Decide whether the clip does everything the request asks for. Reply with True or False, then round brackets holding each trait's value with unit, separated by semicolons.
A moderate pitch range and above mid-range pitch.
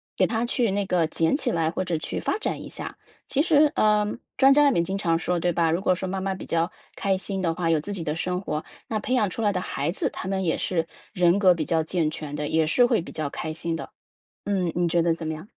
False (3.6 semitones; 180 Hz)